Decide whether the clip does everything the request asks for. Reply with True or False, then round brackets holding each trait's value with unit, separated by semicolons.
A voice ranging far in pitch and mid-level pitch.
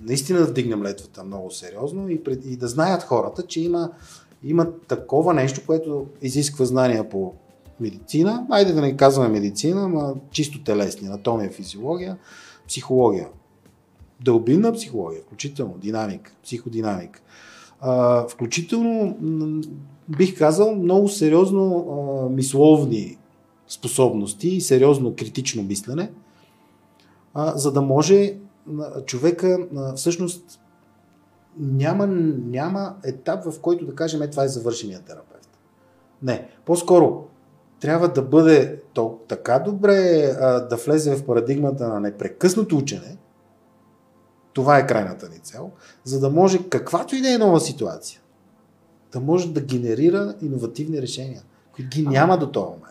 True (5.9 semitones; 145 Hz)